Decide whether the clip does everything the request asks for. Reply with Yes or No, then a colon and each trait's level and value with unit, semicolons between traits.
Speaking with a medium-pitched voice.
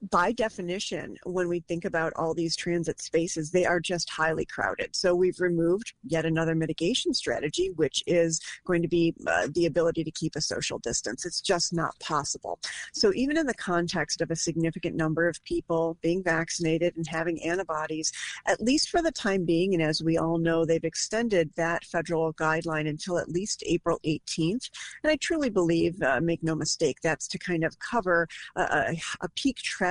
Yes: medium, 170 Hz